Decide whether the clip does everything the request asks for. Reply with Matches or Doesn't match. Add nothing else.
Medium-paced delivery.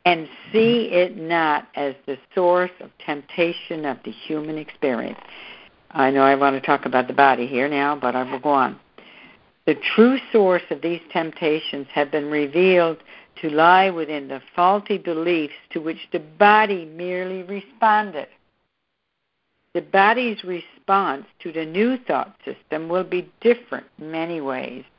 Matches